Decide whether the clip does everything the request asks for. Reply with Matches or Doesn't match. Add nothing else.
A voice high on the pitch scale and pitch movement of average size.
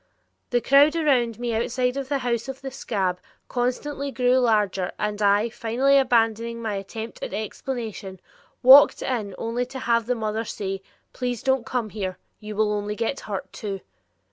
Matches